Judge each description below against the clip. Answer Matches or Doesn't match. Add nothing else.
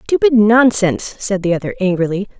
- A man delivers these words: Doesn't match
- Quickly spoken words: Doesn't match